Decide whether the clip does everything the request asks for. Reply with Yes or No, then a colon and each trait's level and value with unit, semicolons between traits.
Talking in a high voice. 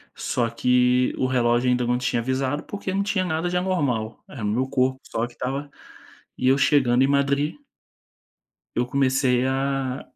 No: low, 130 Hz